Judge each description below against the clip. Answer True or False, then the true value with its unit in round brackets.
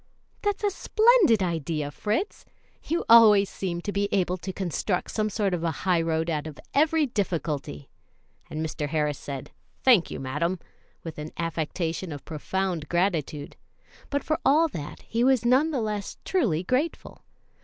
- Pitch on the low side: False (185 Hz)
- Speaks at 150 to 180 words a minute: True (155 wpm)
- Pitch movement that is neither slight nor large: False (6.7 semitones)